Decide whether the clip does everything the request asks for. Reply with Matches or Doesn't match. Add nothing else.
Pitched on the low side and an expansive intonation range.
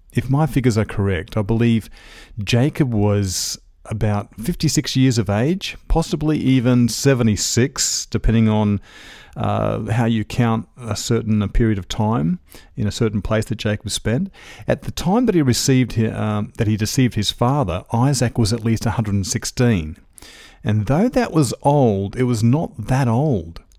Doesn't match